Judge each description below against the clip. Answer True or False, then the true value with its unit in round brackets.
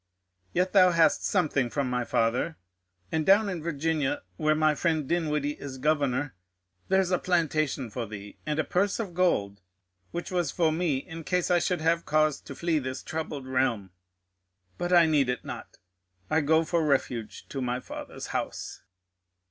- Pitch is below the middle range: False (155 Hz)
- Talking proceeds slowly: False (170 wpm)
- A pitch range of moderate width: True (4.3 semitones)